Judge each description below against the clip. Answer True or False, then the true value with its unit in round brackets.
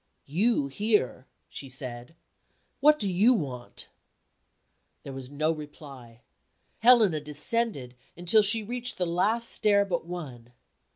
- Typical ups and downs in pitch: False (8.0 semitones)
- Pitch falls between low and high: True (170 Hz)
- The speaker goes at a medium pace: False (120 wpm)